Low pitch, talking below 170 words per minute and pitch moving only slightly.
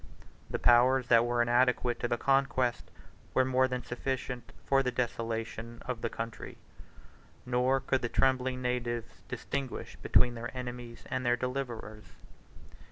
Yes: low, 125 Hz; average, 140 wpm; narrow, 1.5 semitones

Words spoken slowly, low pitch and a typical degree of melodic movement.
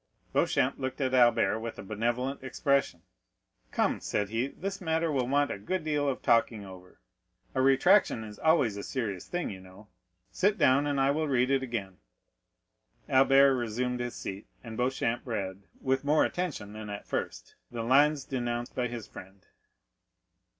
No: average, 165 wpm; low, 125 Hz; average, 4.2 semitones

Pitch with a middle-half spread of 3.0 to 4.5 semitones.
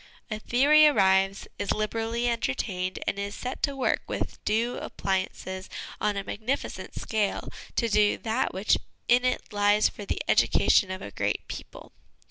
Yes: average, 3.4 semitones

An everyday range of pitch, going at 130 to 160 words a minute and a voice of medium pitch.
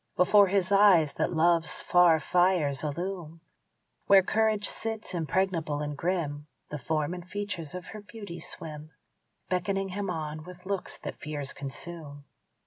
Yes: average, 4.0 semitones; average, 140 wpm; medium, 175 Hz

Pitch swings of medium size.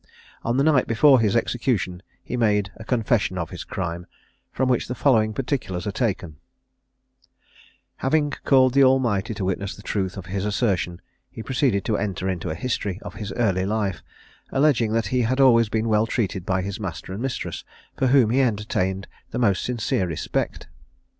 Yes: average, 4.6 semitones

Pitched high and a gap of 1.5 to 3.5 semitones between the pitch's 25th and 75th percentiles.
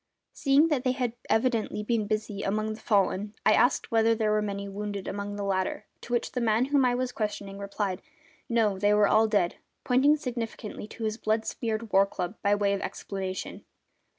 Yes: high, 215 Hz; narrow, 2.6 semitones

